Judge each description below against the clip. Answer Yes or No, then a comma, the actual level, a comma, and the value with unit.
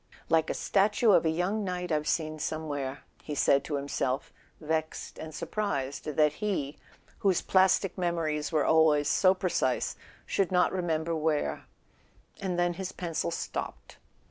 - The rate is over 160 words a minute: No, average, 150 wpm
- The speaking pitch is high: No, medium, 160 Hz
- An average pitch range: Yes, average, 3.3 semitones